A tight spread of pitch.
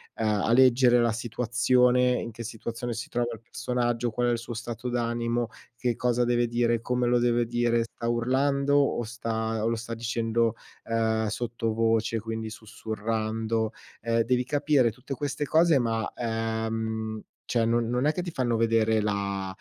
Yes: narrow, 1.5 semitones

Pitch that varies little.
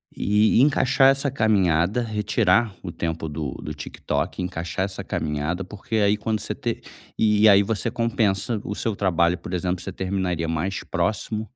No: average, 3.8 semitones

